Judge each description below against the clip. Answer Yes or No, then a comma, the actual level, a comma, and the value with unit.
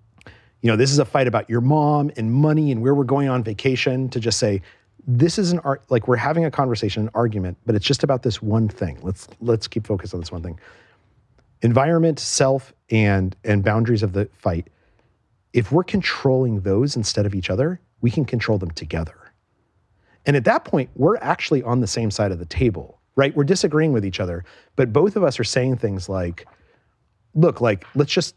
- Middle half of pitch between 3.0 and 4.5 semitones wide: No, average, 4.9 semitones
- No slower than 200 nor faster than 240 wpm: Yes, fast, 205 wpm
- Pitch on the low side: Yes, low, 115 Hz